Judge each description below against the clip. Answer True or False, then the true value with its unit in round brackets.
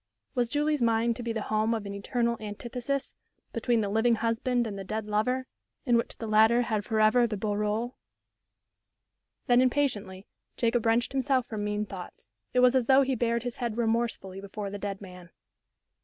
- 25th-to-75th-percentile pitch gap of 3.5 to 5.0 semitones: False (2.7 semitones)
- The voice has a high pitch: True (230 Hz)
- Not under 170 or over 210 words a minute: True (185 wpm)